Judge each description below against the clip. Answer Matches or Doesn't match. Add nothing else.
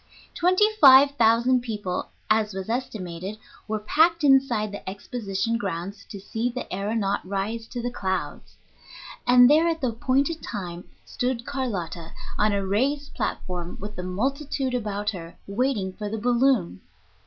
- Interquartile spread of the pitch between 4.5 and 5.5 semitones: Matches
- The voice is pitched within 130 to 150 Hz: Doesn't match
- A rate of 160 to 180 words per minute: Doesn't match